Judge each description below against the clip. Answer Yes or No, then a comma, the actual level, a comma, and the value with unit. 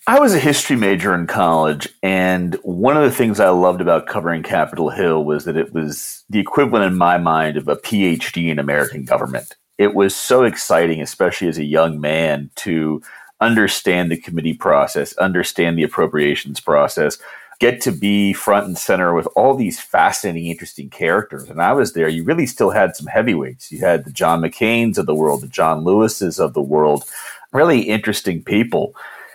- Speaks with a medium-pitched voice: No, very low, 85 Hz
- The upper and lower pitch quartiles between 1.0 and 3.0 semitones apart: No, average, 3.6 semitones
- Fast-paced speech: No, average, 185 wpm